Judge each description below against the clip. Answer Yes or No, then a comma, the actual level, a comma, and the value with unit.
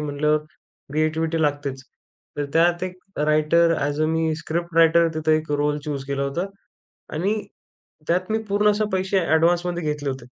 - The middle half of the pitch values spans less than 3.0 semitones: Yes, narrow, 2.5 semitones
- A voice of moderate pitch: Yes, medium, 160 Hz